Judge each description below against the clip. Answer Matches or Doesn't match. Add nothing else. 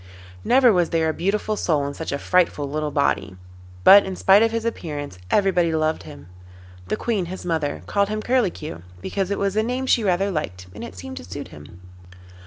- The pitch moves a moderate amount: Doesn't match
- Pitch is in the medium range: Matches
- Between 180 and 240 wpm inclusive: Matches